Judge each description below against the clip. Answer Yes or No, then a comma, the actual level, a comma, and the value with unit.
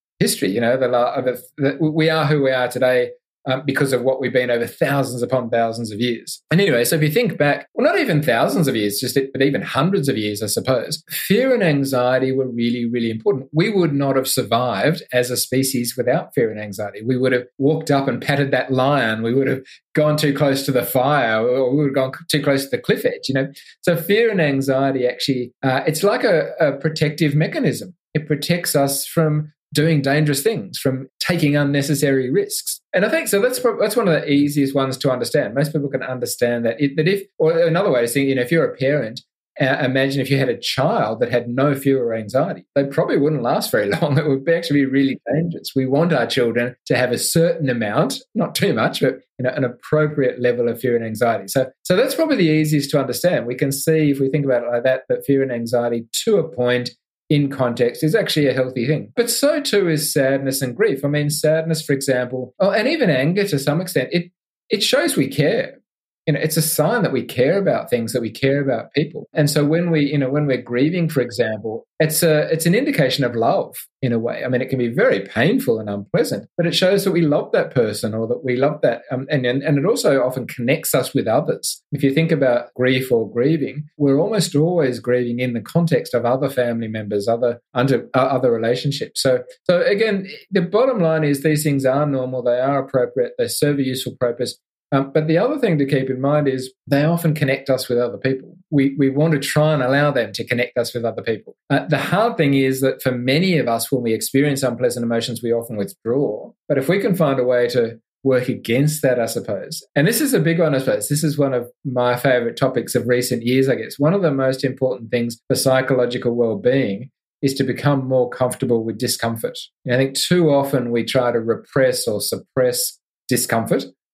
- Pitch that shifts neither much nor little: Yes, average, 3.9 semitones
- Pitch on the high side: No, low, 135 Hz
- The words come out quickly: Yes, fast, 230 wpm